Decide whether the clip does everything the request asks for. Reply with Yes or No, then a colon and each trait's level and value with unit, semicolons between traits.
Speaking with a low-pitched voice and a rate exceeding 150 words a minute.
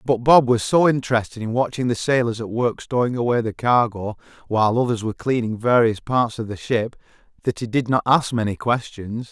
Yes: low, 120 Hz; average, 200 wpm